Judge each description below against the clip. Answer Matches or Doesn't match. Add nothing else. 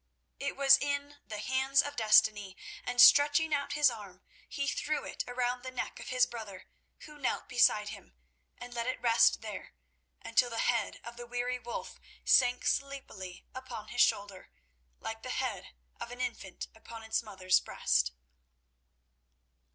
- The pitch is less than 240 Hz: Doesn't match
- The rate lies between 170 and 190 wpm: Doesn't match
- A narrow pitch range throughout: Doesn't match